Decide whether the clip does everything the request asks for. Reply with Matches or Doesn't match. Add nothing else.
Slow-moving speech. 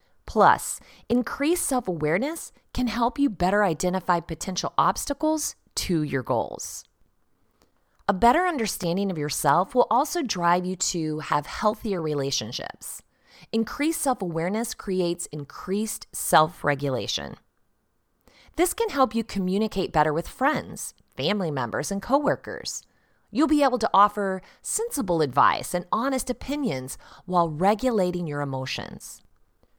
Matches